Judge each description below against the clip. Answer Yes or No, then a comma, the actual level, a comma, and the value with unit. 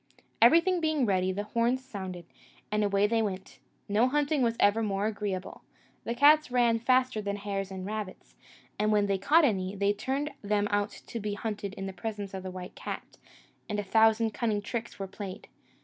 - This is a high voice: Yes, high, 210 Hz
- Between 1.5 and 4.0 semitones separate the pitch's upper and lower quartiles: Yes, average, 3.0 semitones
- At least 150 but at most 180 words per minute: No, average, 195 wpm